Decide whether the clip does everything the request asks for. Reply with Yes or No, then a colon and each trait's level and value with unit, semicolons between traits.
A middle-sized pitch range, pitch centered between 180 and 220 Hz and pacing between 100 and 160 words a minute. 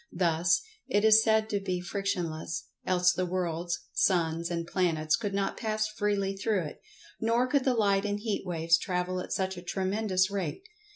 No: average, 3.1 semitones; medium, 185 Hz; average, 175 wpm